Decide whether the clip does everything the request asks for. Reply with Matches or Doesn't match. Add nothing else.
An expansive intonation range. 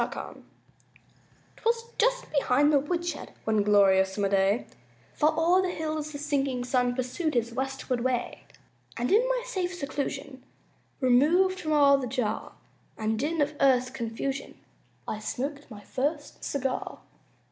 Doesn't match